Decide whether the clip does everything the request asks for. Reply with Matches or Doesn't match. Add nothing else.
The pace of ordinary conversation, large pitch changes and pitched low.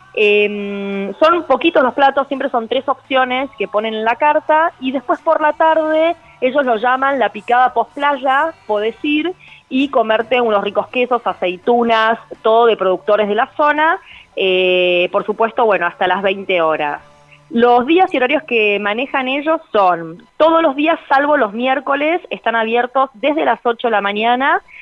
Doesn't match